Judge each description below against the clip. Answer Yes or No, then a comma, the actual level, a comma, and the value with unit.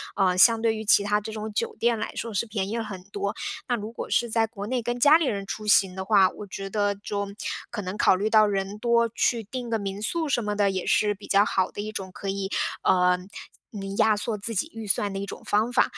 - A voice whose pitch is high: Yes, high, 210 Hz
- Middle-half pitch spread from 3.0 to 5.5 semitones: No, narrow, 2.4 semitones